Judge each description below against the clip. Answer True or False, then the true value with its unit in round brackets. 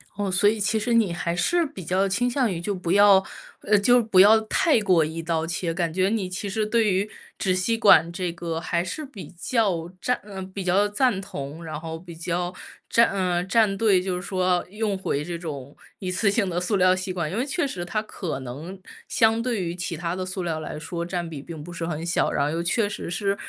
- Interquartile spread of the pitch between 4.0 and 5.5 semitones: False (3.4 semitones)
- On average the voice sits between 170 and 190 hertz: True (185 Hz)